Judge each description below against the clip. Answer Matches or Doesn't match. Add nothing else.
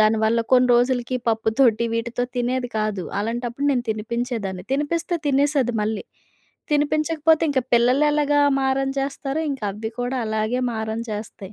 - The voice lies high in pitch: Matches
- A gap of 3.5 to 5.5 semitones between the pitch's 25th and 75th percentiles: Matches